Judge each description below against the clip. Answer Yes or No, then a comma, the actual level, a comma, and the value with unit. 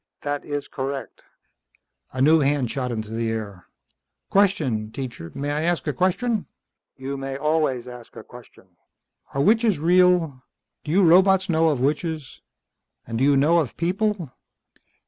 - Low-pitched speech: No, medium, 145 Hz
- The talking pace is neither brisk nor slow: Yes, average, 150 wpm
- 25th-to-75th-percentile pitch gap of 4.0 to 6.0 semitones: Yes, average, 5.1 semitones